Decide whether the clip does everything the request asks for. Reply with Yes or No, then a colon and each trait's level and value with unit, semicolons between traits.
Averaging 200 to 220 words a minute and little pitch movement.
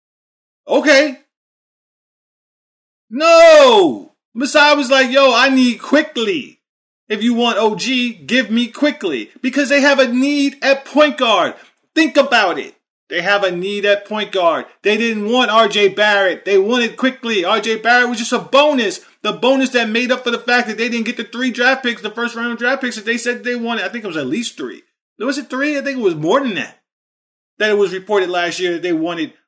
No: fast, 205 wpm; average, 4.5 semitones